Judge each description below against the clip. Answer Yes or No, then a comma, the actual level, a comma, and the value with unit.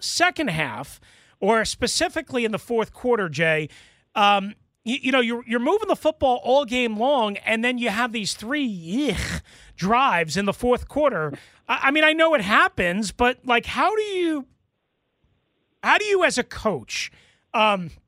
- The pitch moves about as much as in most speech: No, wide, 5.7 semitones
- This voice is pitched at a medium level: No, high, 245 Hz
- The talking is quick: No, average, 175 wpm